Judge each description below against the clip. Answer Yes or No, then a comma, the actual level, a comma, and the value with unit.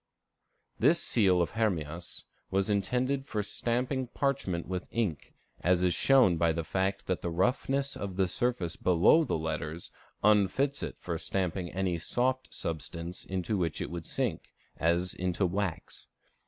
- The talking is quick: No, average, 155 wpm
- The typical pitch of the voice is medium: No, very low, 95 Hz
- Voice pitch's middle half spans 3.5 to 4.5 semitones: No, wide, 5.5 semitones